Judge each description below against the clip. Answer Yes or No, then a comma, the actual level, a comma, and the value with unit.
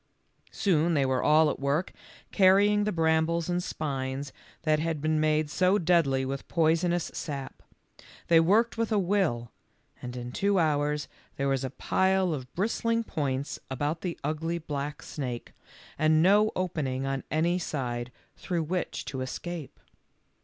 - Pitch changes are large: No, average, 4.5 semitones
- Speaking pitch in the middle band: Yes, medium, 155 Hz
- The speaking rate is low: No, average, 150 wpm